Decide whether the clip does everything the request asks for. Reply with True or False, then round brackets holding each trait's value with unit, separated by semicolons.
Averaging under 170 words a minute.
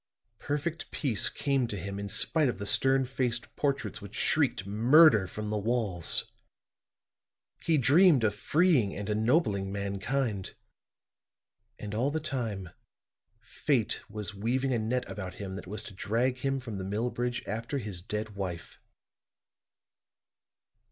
True (140 wpm)